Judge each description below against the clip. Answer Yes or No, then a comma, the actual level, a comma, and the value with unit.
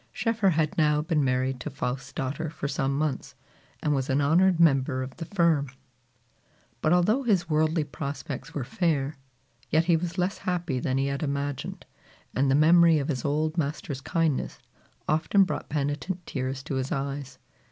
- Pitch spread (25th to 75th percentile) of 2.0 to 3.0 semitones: No, average, 3.4 semitones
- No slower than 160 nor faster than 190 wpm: Yes, average, 170 wpm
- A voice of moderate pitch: Yes, medium, 150 Hz